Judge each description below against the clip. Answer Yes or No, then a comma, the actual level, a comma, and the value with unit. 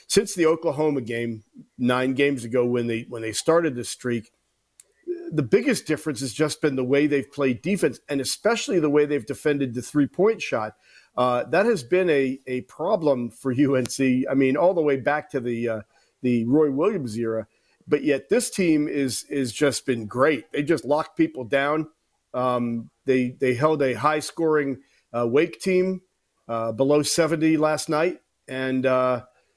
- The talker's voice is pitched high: No, medium, 140 Hz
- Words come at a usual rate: Yes, average, 180 wpm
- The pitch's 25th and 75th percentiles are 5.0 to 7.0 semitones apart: No, average, 3.7 semitones